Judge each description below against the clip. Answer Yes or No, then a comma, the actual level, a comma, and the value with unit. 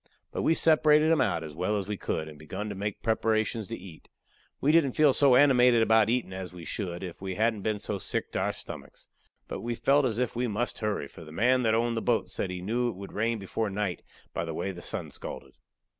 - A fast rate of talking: Yes, fast, 245 wpm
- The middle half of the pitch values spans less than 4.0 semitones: No, average, 4.5 semitones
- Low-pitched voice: Yes, low, 110 Hz